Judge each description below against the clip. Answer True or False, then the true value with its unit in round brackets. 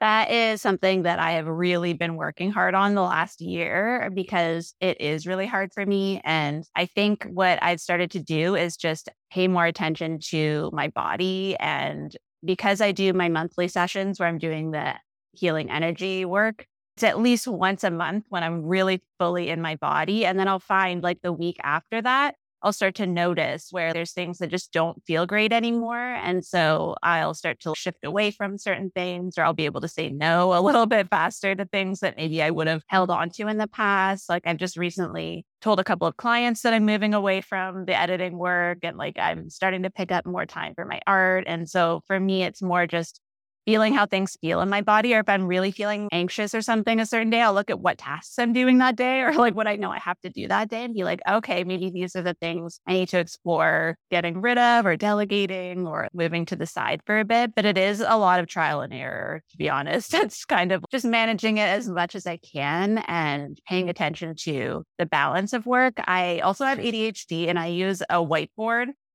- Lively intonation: False (3.4 semitones)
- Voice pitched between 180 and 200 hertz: True (185 Hz)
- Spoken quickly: True (225 wpm)